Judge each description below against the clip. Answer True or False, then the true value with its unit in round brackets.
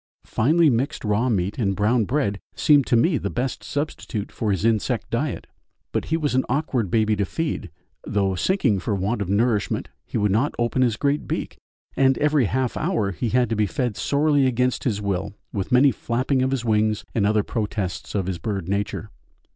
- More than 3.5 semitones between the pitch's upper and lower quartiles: True (4.6 semitones)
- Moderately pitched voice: False (115 Hz)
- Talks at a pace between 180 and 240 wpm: True (195 wpm)